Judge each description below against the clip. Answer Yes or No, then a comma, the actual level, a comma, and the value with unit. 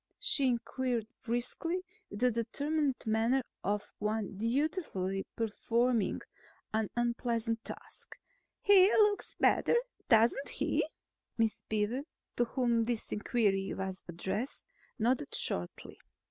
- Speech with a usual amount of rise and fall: Yes, average, 3.4 semitones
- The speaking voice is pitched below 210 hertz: No, high, 235 Hz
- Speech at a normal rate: No, slow, 105 wpm